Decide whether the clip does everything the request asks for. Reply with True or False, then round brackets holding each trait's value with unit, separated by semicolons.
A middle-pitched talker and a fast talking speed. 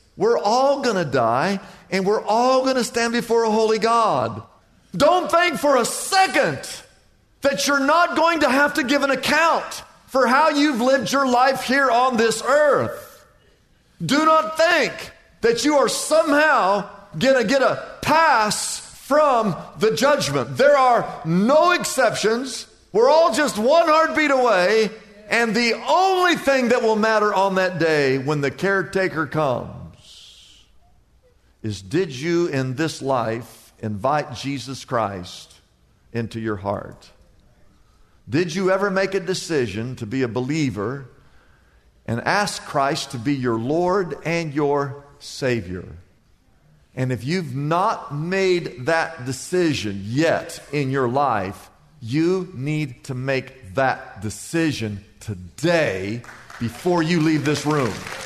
False (180 Hz; 135 wpm)